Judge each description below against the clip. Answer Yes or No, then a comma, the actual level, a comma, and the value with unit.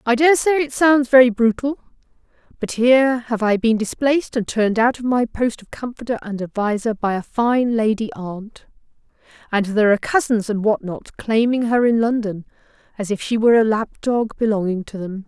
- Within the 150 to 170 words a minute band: No, average, 190 wpm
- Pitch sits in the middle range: No, high, 230 Hz